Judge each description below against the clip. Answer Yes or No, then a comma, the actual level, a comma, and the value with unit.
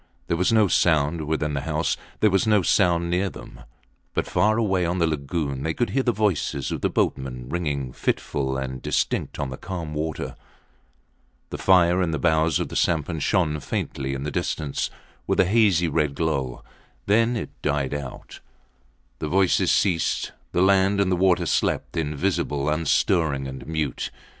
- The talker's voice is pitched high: No, very low, 80 Hz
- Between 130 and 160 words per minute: No, average, 170 wpm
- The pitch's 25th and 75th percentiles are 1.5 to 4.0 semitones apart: No, average, 4.5 semitones